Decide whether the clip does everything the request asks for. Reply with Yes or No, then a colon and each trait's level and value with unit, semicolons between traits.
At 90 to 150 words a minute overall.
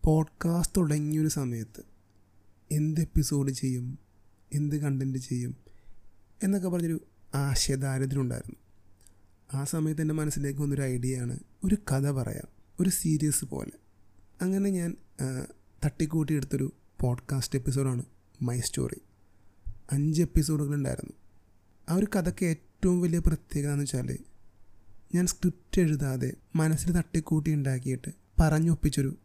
Yes: average, 105 wpm